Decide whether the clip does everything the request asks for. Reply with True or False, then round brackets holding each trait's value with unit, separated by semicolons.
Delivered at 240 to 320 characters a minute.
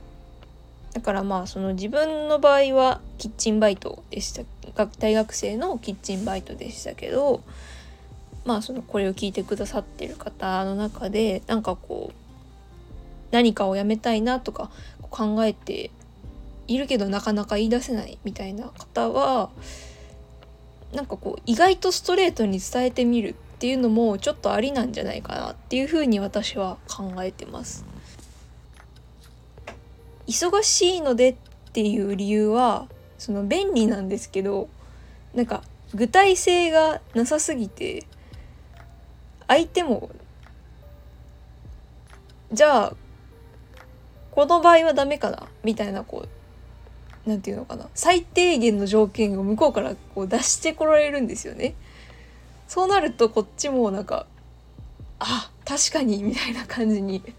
True (250 characters per minute)